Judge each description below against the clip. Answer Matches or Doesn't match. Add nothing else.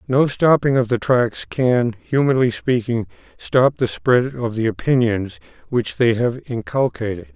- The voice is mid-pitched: Doesn't match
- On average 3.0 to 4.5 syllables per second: Matches